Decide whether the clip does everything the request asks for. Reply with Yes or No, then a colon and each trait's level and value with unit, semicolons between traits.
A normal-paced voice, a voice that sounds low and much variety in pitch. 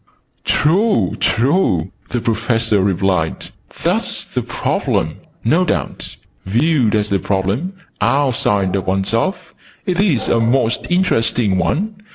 No: slow, 115 wpm; low, 115 Hz; wide, 8.2 semitones